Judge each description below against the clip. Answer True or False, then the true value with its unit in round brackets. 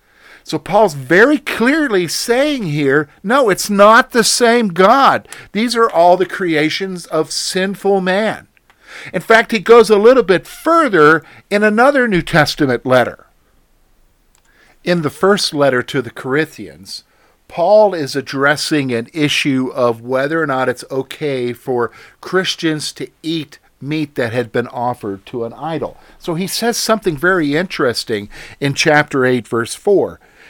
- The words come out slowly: False (145 wpm)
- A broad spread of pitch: True (7.2 semitones)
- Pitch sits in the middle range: True (160 Hz)